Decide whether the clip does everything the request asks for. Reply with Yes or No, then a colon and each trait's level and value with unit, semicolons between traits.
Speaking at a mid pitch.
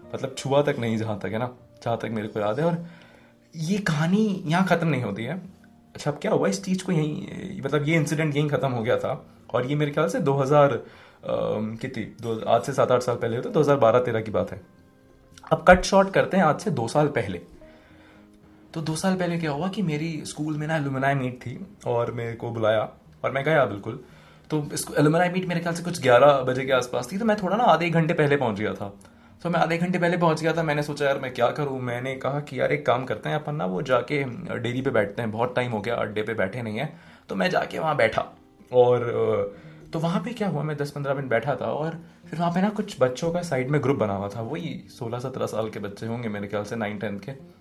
Yes: medium, 145 Hz